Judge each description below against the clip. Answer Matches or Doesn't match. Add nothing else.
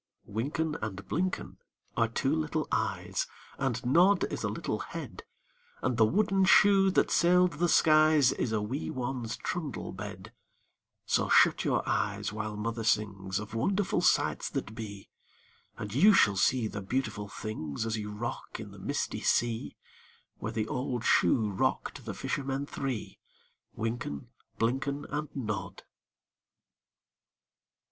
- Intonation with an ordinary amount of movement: Doesn't match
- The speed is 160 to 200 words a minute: Doesn't match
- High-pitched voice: Doesn't match